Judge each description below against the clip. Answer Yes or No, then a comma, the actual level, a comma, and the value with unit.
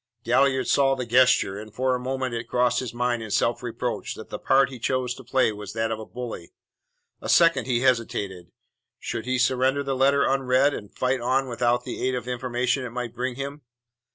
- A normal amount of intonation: No, narrow, 1.9 semitones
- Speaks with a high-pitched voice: No, low, 125 Hz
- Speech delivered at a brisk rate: Yes, fast, 210 wpm